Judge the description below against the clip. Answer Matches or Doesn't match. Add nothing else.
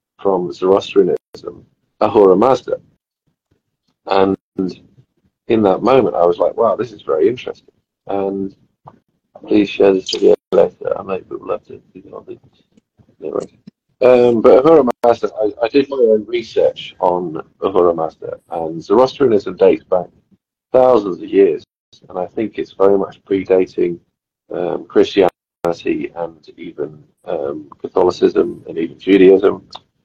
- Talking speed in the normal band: Doesn't match